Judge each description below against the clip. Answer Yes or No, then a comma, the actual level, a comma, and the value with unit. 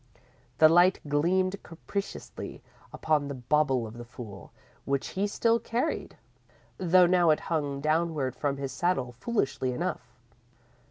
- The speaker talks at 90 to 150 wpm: Yes, average, 140 wpm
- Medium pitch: Yes, medium, 155 Hz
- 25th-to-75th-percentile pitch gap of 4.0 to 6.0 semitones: Yes, wide, 5.4 semitones